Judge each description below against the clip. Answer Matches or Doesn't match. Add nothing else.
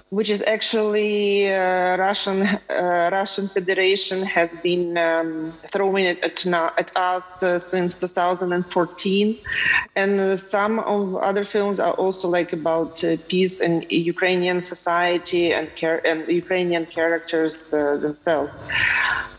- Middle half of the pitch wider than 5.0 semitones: Doesn't match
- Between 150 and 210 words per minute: Doesn't match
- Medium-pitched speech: Matches